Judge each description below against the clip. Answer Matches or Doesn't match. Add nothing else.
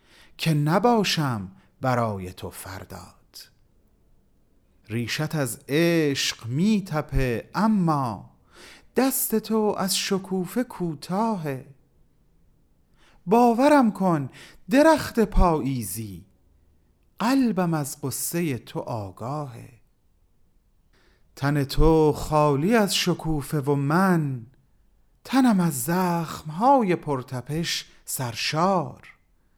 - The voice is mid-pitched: Matches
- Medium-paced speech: Doesn't match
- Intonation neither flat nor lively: Doesn't match